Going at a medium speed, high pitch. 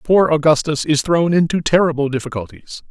No: average, 145 wpm; medium, 155 Hz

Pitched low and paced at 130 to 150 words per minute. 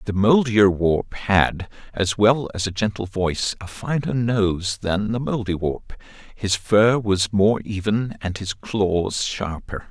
Yes: low, 105 Hz; average, 145 wpm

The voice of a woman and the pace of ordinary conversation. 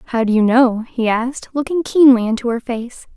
No: female; fast, 210 wpm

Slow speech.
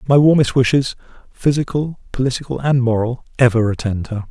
Yes: slow, 110 wpm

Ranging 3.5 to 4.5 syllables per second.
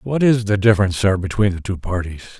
No: 6.2 syllables/s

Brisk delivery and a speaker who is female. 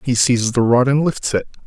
No: fast, 255 wpm; male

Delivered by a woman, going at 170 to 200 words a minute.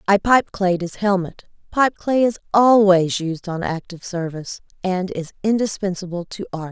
No: female; slow, 135 wpm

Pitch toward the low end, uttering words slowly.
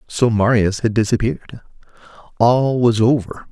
Yes: low, 115 Hz; slow, 120 wpm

